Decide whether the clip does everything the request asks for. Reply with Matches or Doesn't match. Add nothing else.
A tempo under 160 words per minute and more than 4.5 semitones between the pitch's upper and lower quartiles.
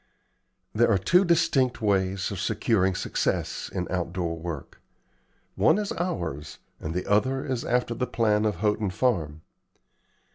Matches